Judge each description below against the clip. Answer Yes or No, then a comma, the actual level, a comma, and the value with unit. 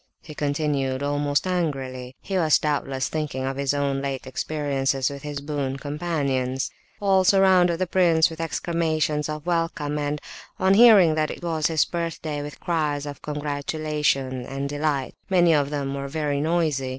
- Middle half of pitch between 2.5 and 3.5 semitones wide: Yes, average, 2.9 semitones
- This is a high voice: No, medium, 150 Hz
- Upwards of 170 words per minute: No, average, 160 wpm